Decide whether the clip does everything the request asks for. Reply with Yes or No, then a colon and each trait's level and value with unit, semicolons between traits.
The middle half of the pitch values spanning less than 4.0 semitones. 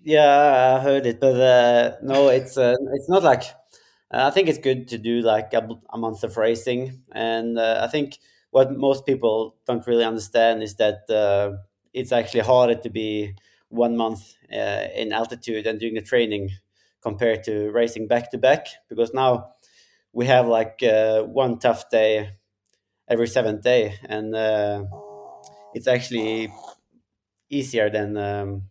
Yes: average, 2.8 semitones